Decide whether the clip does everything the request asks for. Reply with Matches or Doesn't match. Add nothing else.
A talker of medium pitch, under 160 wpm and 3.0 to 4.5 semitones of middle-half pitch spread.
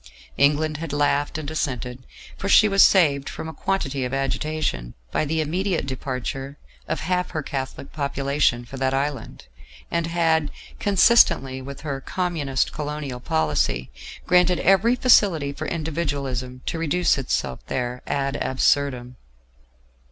Matches